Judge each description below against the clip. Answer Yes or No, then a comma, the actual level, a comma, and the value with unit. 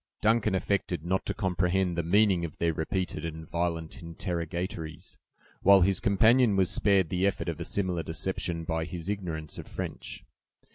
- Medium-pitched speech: No, very low, 90 Hz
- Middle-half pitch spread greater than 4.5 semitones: No, average, 2.7 semitones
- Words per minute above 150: Yes, average, 160 wpm